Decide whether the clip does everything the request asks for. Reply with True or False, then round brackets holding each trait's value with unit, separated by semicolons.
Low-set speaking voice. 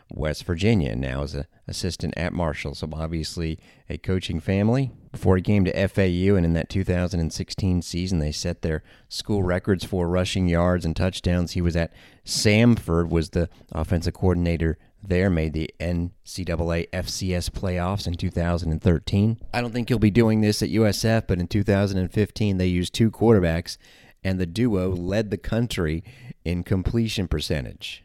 True (90 Hz)